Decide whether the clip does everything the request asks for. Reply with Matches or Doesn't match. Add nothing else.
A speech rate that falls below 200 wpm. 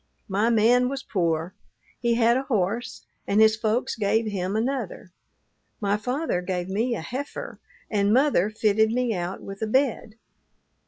Matches